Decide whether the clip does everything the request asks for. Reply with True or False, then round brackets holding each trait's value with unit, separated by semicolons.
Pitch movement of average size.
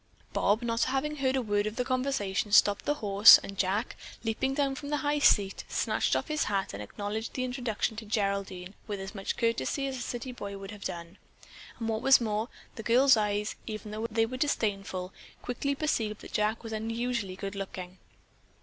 True (3.9 semitones)